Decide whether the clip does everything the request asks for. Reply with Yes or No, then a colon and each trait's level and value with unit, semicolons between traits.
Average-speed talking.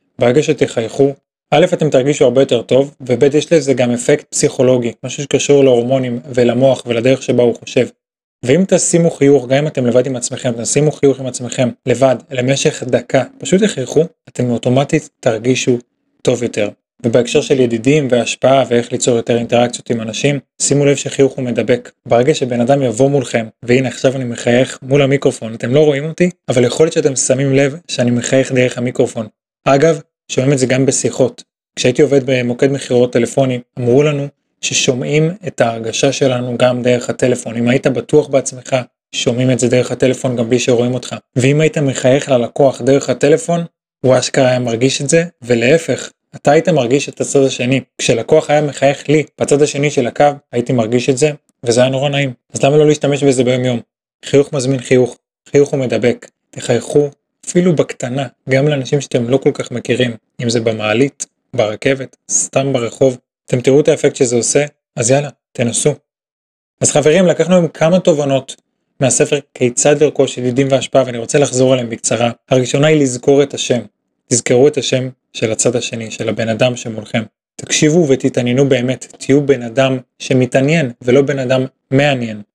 No: fast, 160 wpm